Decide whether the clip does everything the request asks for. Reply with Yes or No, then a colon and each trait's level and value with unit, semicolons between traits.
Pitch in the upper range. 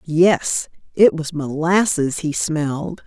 No: medium, 160 Hz